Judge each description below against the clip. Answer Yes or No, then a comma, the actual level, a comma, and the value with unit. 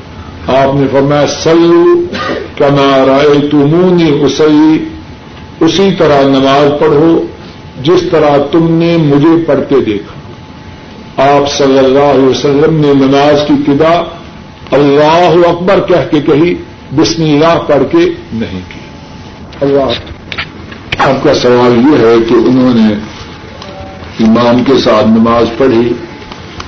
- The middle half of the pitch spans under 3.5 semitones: No, average, 5.0 semitones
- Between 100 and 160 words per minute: Yes, average, 115 wpm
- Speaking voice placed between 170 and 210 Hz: No, medium, 140 Hz